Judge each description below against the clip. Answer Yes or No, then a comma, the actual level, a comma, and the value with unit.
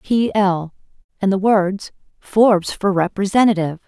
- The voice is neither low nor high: No, high, 195 Hz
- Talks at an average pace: No, slow, 125 wpm